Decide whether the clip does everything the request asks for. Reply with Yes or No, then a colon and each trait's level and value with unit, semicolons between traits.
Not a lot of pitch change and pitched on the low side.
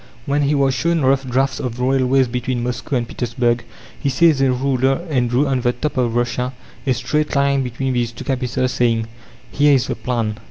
Yes: narrow, 2.0 semitones; low, 130 Hz